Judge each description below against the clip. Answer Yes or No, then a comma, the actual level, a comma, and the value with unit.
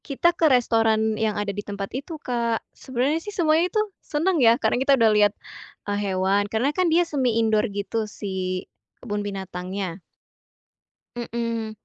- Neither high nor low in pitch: No, high, 225 Hz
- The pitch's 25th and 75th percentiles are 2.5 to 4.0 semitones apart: No, average, 5.0 semitones